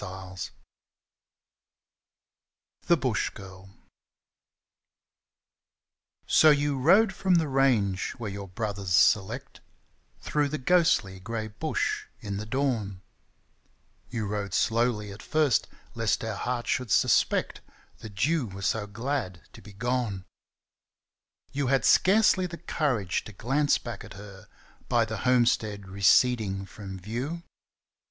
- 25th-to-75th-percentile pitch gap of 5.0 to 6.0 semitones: Yes, wide, 5.4 semitones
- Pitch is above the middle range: No, low, 110 Hz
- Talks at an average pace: No, slow, 120 wpm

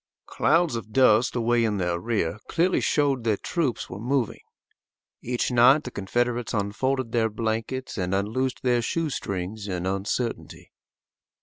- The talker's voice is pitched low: Yes, low, 115 Hz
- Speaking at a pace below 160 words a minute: Yes, average, 140 wpm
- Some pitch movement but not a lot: Yes, average, 4.1 semitones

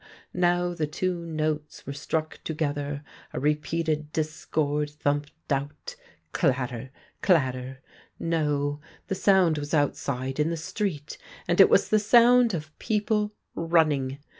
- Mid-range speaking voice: Yes, medium, 155 Hz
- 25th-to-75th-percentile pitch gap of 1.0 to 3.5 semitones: Yes, average, 2.7 semitones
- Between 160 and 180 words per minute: No, slow, 135 wpm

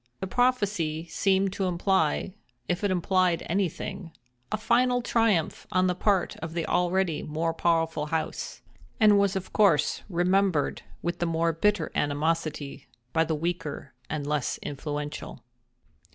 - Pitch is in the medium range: Yes, medium, 170 Hz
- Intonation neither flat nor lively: Yes, average, 3.6 semitones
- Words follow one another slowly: Yes, slow, 130 wpm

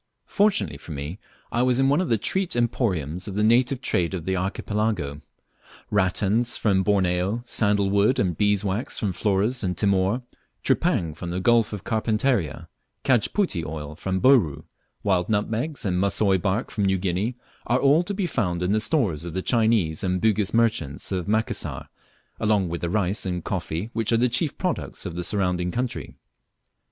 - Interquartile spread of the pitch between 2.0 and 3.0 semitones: No, average, 4.5 semitones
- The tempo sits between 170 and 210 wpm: Yes, average, 175 wpm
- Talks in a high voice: No, low, 100 Hz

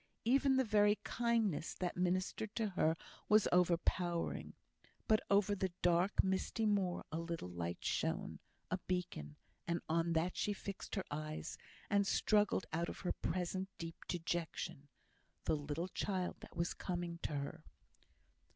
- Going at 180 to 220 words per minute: No, average, 145 wpm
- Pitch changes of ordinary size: Yes, average, 3.3 semitones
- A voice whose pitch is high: No, medium, 180 Hz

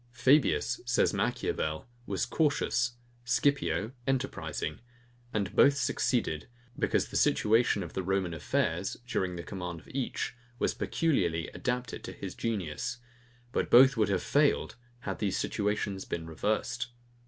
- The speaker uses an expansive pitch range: Yes, wide, 5.8 semitones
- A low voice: Yes, low, 110 Hz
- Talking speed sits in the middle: No, slow, 130 wpm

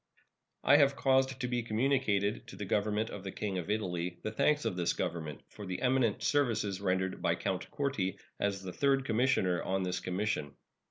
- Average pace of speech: Yes, average, 185 wpm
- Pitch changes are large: Yes, wide, 5.7 semitones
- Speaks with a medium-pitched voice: No, low, 105 Hz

